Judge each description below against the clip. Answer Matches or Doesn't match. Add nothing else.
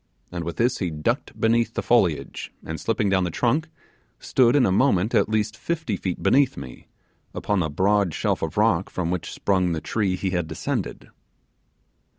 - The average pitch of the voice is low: Matches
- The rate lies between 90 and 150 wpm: Doesn't match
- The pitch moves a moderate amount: Matches